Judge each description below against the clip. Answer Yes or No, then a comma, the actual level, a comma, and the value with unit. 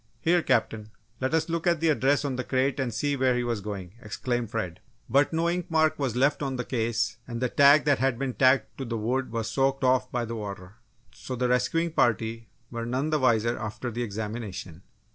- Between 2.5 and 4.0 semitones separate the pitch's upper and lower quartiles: Yes, average, 3.6 semitones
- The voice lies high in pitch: No, low, 125 Hz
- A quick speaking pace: Yes, fast, 220 wpm